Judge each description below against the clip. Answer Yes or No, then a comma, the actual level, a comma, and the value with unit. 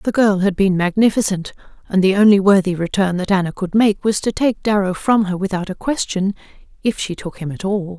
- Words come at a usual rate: No, fast, 220 wpm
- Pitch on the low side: No, high, 195 Hz